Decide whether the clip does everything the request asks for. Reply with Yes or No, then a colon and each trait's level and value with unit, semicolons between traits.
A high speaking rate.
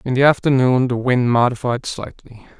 No: average, 160 wpm